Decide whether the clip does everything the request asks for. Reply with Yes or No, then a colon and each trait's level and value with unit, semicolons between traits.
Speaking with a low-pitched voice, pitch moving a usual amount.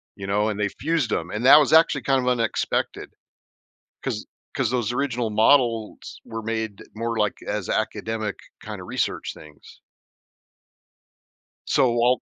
Yes: low, 115 Hz; average, 3.0 semitones